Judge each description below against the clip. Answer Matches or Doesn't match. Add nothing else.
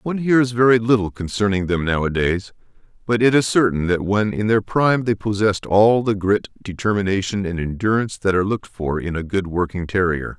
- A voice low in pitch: Matches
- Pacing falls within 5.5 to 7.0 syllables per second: Matches